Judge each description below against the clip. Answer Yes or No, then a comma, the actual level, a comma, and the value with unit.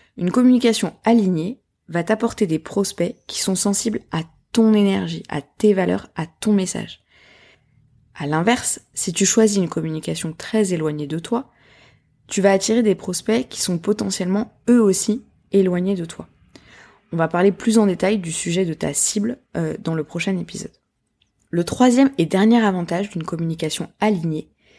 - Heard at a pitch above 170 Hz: Yes, high, 190 Hz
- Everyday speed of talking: Yes, average, 160 wpm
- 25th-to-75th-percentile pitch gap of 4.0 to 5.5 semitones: Yes, average, 4.6 semitones